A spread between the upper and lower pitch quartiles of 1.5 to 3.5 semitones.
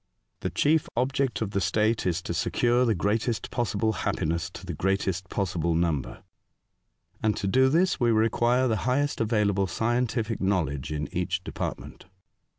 No: average, 4.8 semitones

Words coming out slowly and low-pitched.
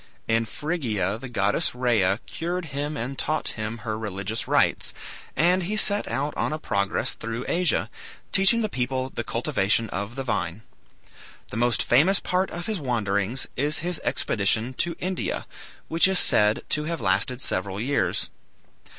No: average, 160 wpm; low, 125 Hz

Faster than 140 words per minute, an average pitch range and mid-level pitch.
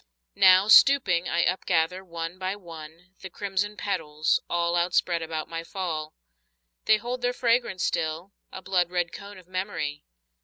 Yes: average, 150 wpm; average, 3.0 semitones; medium, 180 Hz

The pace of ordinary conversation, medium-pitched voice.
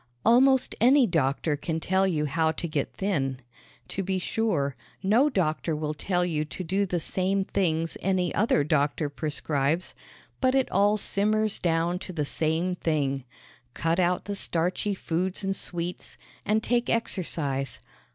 Yes: average, 150 wpm; medium, 175 Hz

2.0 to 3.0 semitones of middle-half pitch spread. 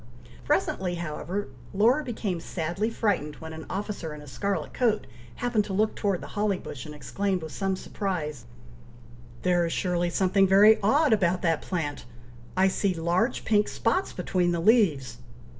No: average, 3.8 semitones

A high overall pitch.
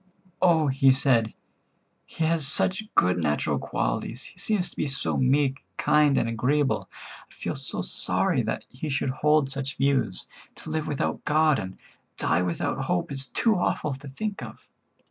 No: low, 135 Hz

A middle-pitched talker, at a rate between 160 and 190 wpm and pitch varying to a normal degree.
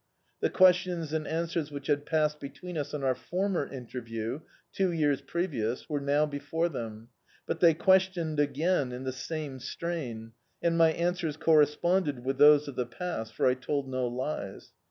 Yes: medium, 150 Hz; average, 175 wpm; average, 4.3 semitones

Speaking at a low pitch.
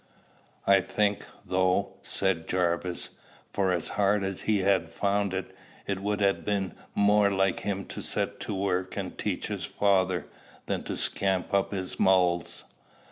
Yes: very low, 95 Hz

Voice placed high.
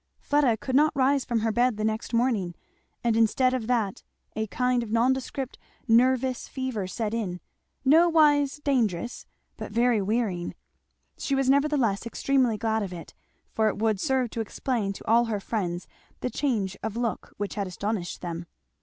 Yes: high, 230 Hz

